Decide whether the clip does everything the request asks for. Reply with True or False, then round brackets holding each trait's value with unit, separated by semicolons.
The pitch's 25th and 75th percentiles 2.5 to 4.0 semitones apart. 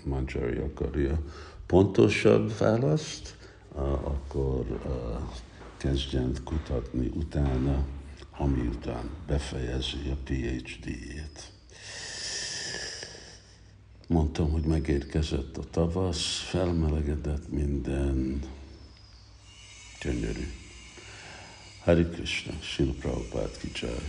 False (5.1 semitones)